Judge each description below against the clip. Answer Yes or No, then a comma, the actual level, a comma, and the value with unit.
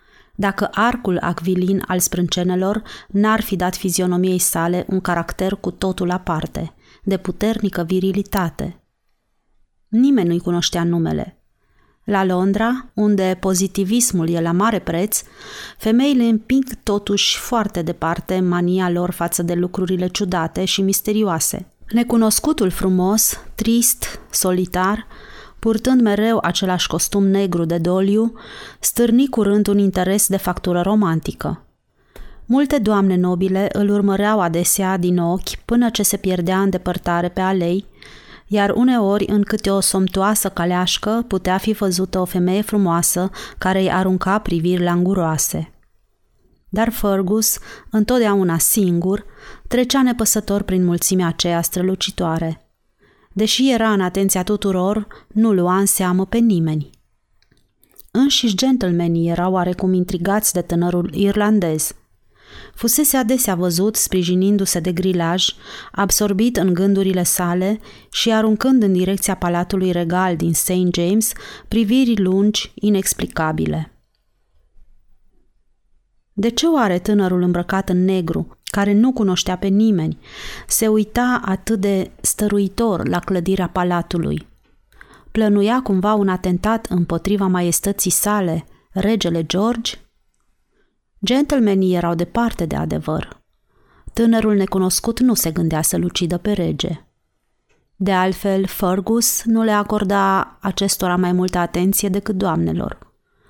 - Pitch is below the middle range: No, high, 190 Hz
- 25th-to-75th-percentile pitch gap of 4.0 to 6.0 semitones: No, average, 2.9 semitones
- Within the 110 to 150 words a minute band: Yes, slow, 115 wpm